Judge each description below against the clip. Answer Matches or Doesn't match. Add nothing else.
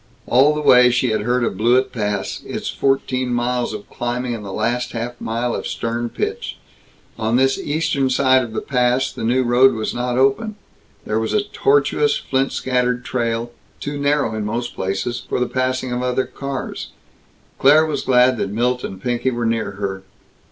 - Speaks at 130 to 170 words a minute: Doesn't match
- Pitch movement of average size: Doesn't match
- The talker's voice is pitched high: Doesn't match